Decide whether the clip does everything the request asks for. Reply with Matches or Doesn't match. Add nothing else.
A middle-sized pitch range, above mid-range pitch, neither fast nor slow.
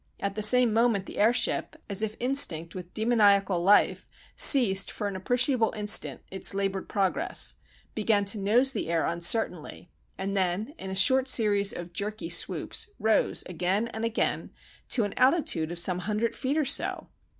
Matches